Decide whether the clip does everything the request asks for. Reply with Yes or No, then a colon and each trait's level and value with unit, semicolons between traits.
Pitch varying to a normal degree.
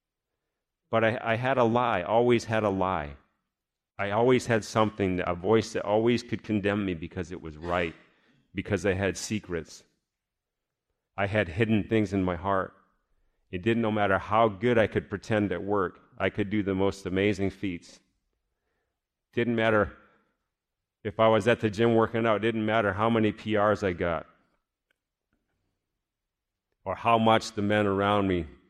Yes: average, 3.0 semitones